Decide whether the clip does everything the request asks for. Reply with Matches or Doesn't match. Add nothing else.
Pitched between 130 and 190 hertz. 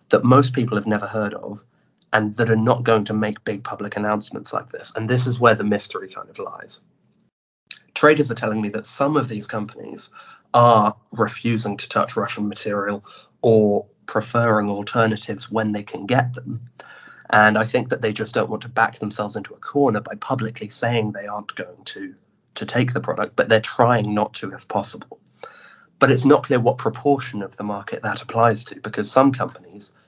Doesn't match